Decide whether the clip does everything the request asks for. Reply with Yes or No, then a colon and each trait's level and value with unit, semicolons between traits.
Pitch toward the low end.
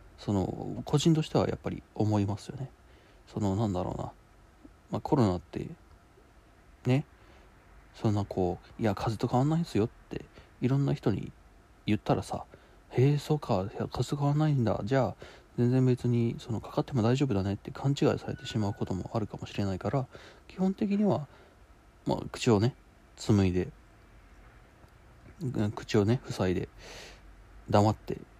Yes: low, 115 Hz